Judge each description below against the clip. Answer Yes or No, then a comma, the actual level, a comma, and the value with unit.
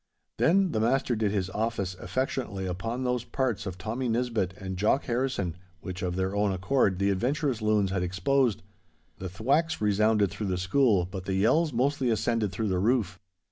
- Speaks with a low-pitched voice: Yes, low, 105 Hz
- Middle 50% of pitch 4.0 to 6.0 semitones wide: Yes, average, 4.8 semitones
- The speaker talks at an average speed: Yes, average, 180 wpm